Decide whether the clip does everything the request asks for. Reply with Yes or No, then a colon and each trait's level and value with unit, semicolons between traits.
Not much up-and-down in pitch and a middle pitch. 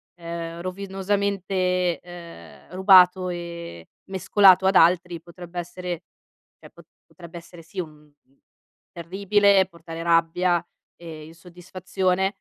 Yes: narrow, 2.0 semitones; medium, 175 Hz